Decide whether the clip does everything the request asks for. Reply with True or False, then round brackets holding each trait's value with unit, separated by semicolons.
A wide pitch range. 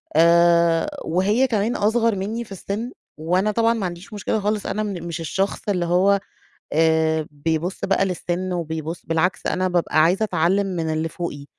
False (3.6 semitones)